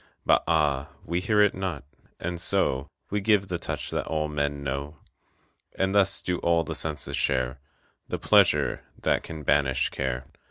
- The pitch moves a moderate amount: Yes, average, 4.5 semitones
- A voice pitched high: No, very low, 80 Hz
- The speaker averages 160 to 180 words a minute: Yes, average, 165 wpm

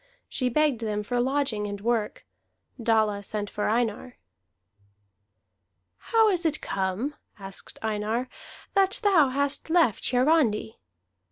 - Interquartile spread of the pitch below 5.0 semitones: No, wide, 5.5 semitones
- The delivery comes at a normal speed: No, slow, 115 wpm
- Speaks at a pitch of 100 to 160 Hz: No, high, 240 Hz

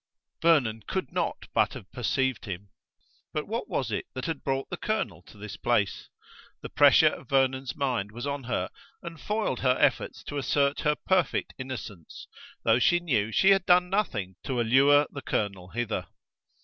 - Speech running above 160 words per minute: Yes, average, 175 wpm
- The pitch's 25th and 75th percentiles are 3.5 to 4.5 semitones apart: No, average, 5.1 semitones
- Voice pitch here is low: Yes, low, 130 Hz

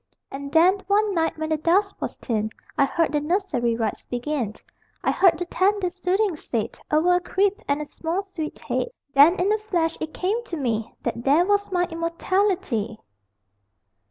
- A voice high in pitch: Yes, very high, 335 Hz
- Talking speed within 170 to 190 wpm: Yes, average, 180 wpm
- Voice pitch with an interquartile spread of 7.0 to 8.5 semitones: No, average, 5.1 semitones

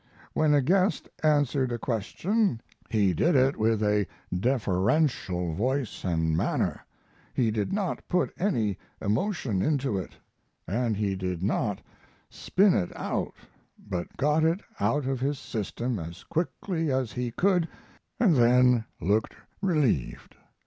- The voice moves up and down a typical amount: No, wide, 6.9 semitones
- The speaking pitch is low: Yes, low, 125 Hz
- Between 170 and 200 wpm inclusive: No, slow, 135 wpm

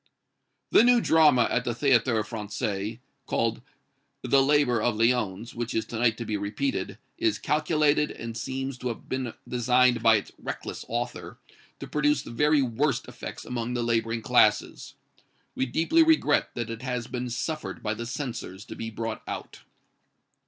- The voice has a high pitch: No, low, 120 Hz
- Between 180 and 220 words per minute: No, average, 165 wpm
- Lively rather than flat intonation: No, average, 3.4 semitones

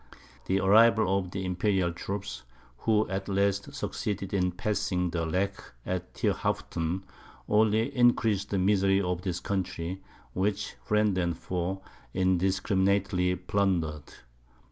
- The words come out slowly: Yes, slow, 120 wpm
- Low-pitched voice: Yes, very low, 95 Hz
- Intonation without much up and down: Yes, narrow, 2.0 semitones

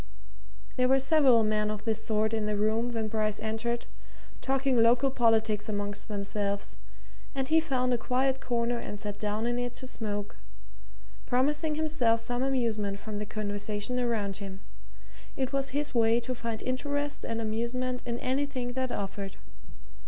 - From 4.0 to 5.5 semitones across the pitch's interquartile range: No, average, 3.2 semitones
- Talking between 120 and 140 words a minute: No, average, 160 wpm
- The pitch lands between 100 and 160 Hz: No, high, 235 Hz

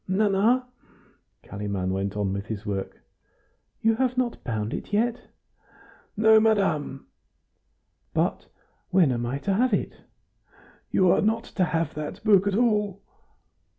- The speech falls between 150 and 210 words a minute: No, slow, 135 wpm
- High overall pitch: Yes, high, 195 Hz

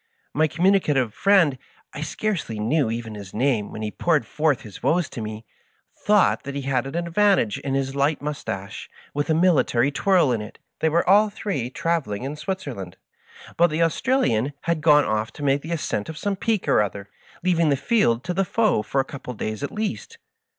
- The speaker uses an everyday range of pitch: No, wide, 6.6 semitones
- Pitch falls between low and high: Yes, medium, 145 Hz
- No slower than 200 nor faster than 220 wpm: Yes, fast, 205 wpm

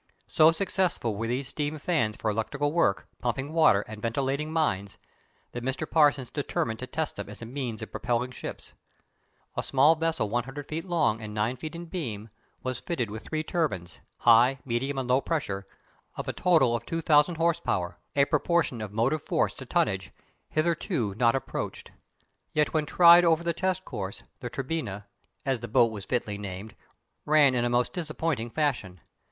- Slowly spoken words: No, average, 175 wpm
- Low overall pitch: Yes, low, 130 Hz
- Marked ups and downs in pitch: Yes, wide, 5.7 semitones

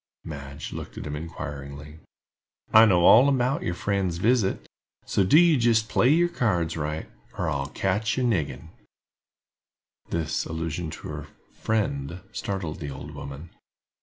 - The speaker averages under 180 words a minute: Yes, average, 145 wpm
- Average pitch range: No, wide, 6.7 semitones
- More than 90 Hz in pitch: No, very low, 85 Hz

